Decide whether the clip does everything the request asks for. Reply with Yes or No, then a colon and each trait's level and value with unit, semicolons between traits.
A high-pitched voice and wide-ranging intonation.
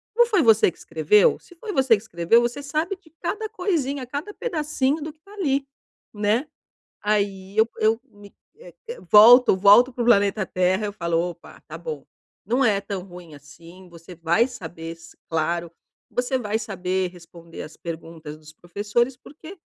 Yes: high, 210 Hz; wide, 7.6 semitones